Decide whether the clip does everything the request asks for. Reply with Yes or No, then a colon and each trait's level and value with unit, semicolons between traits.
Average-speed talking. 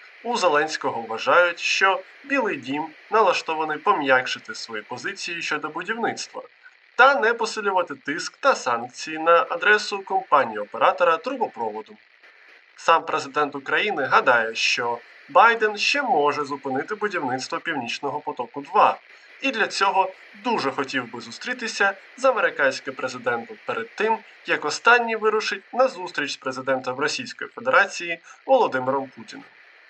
Yes: average, 115 wpm